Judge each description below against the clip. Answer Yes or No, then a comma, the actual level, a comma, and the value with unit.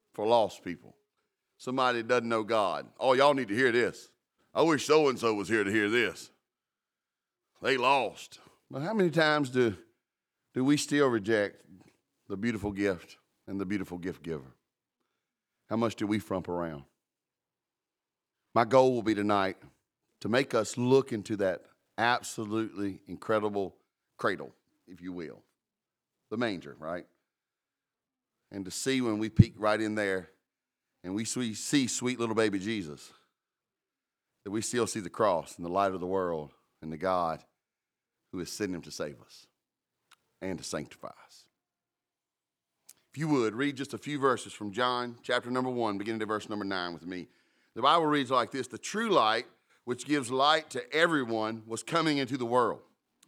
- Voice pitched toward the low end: Yes, low, 115 Hz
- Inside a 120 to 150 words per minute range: No, average, 170 wpm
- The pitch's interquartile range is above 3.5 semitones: Yes, average, 4.2 semitones